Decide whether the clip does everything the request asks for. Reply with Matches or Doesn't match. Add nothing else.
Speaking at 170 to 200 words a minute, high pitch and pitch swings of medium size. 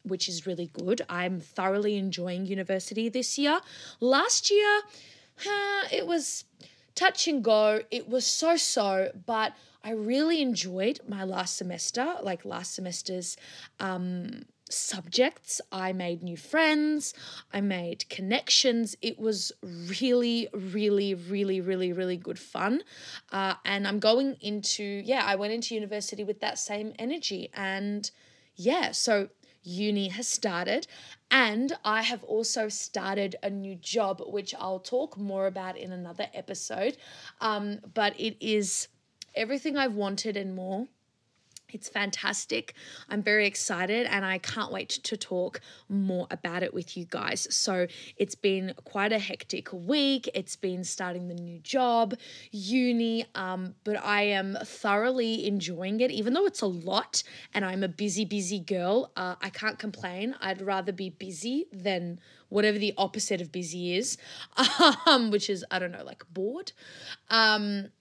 Doesn't match